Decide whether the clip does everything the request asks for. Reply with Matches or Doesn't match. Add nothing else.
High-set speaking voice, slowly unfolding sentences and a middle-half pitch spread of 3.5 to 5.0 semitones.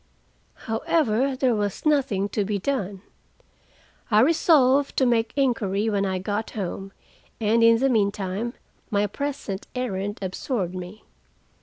Matches